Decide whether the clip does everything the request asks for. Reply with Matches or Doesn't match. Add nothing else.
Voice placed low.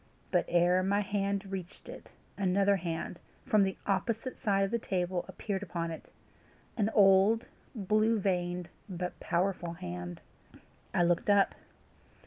Doesn't match